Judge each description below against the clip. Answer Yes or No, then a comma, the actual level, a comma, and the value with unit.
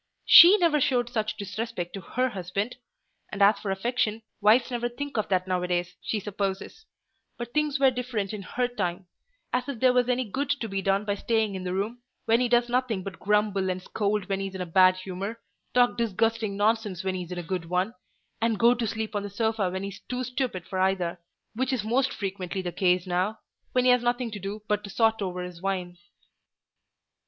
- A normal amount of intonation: Yes, average, 4.3 semitones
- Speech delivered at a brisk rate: Yes, fast, 215 wpm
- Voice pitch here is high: Yes, high, 210 Hz